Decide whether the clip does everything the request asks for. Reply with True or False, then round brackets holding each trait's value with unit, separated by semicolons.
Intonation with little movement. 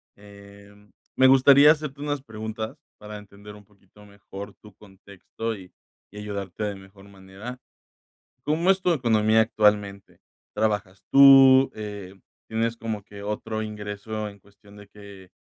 True (2.0 semitones)